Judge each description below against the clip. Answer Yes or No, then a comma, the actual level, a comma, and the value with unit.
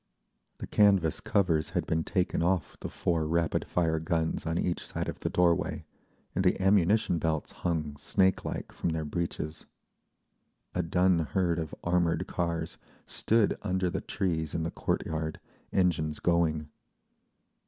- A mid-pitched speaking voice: No, very low, 85 Hz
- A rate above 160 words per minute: No, average, 145 wpm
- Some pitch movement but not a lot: No, narrow, 2.2 semitones